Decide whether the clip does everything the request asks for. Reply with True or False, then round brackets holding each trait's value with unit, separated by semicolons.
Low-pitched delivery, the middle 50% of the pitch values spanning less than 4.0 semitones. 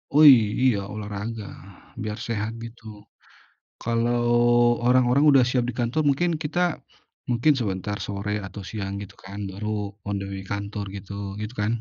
True (110 Hz; 3.2 semitones)